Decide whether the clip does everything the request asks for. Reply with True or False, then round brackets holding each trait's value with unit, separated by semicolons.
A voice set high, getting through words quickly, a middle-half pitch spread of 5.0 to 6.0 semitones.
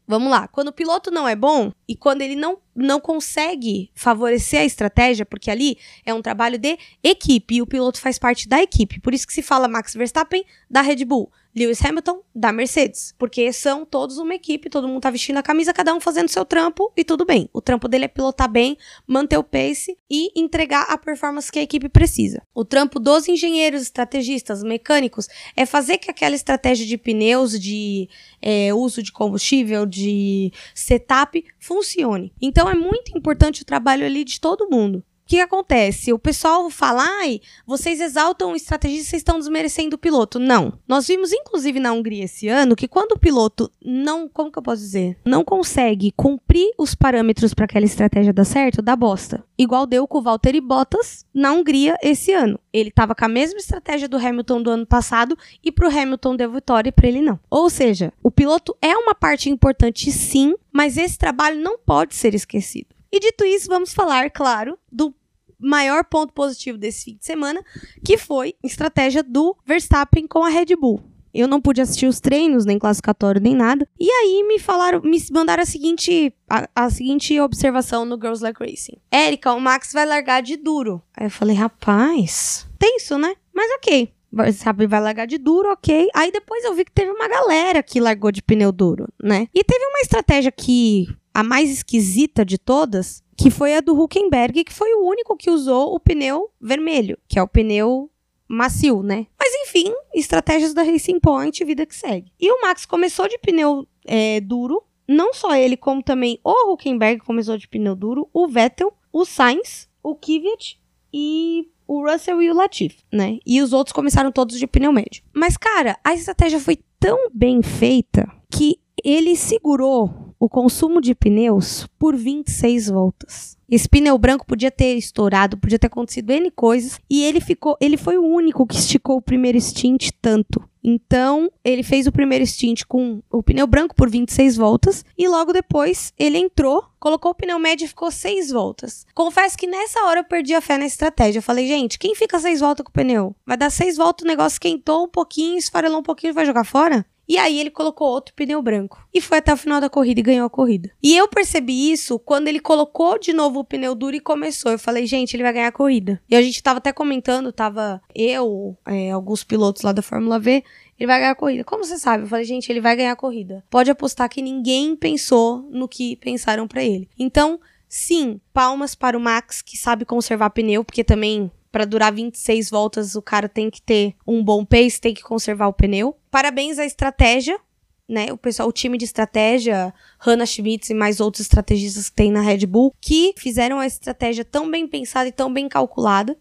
True (270 Hz; 200 wpm; 5.4 semitones)